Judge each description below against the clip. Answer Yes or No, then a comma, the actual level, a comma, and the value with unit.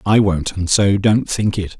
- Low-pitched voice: Yes, low, 100 Hz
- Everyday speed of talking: No, fast, 235 wpm